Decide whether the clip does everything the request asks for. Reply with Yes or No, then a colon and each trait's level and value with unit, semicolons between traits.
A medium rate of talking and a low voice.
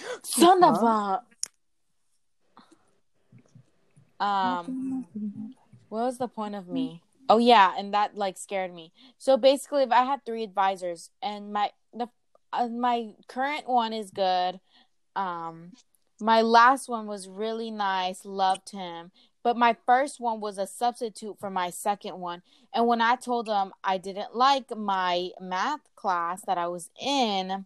No: average, 150 wpm; high, 220 Hz